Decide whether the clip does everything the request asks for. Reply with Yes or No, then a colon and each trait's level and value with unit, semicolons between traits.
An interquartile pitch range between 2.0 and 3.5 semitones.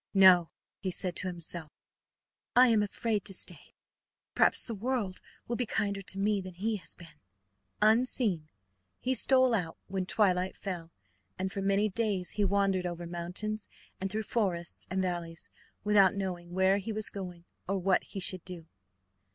Yes: average, 2.9 semitones